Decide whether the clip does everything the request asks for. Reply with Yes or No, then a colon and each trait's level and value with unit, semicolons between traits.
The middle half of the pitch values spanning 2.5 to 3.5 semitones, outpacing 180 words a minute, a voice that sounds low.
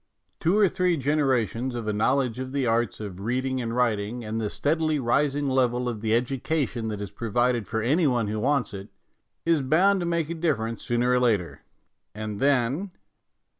No: average, 4.3 semitones; average, 195 wpm; low, 125 Hz